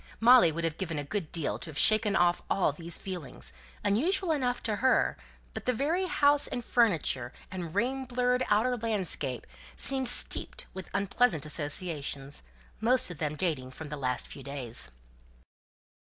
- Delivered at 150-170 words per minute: Yes, average, 160 wpm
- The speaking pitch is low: No, high, 190 Hz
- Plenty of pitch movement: Yes, wide, 8.5 semitones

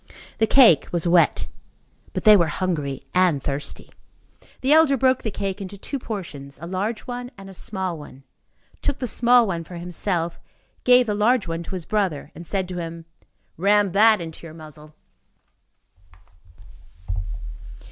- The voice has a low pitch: No, medium, 185 Hz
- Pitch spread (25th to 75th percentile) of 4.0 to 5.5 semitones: Yes, average, 4.7 semitones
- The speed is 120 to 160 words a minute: Yes, average, 155 wpm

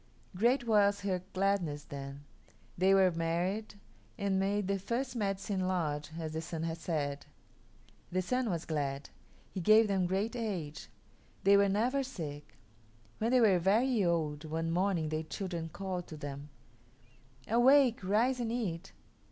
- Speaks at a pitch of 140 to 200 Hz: Yes, high, 190 Hz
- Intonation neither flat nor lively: Yes, average, 4.7 semitones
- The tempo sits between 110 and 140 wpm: No, average, 150 wpm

